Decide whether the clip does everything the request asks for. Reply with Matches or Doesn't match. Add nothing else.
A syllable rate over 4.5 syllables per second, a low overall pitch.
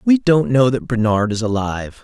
Matches